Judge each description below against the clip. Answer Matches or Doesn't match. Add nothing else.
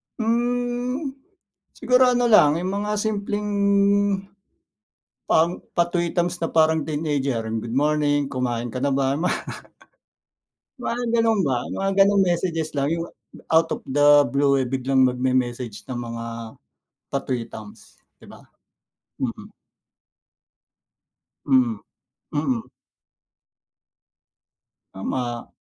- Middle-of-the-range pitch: Matches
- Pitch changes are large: Matches